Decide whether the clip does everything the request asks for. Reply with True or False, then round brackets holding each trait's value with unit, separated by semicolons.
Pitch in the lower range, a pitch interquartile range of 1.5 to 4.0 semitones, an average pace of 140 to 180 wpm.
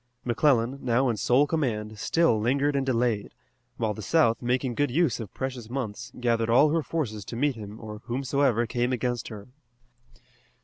True (120 Hz; 3.4 semitones; 170 wpm)